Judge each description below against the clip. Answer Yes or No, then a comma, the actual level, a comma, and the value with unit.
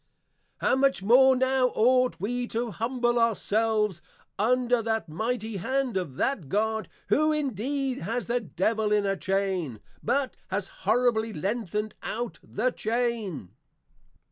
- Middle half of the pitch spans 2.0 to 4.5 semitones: Yes, average, 3.5 semitones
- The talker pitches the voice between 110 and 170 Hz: No, high, 225 Hz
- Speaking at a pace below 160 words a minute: Yes, average, 140 wpm